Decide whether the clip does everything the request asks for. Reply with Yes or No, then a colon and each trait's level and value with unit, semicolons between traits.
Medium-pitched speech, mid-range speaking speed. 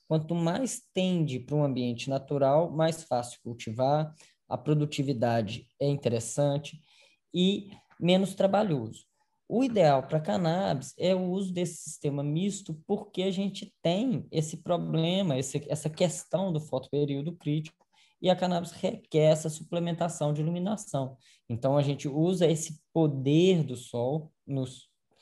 Yes: medium, 160 Hz; average, 135 wpm